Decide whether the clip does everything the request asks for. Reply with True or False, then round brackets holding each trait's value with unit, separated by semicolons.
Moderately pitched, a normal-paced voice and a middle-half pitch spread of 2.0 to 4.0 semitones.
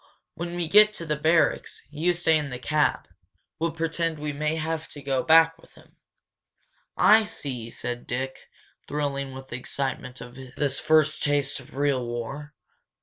True (150 Hz; 165 wpm; 3.4 semitones)